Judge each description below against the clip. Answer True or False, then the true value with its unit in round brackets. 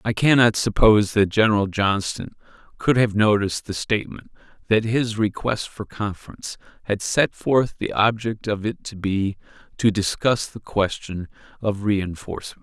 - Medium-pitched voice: False (105 Hz)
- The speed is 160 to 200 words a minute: False (150 wpm)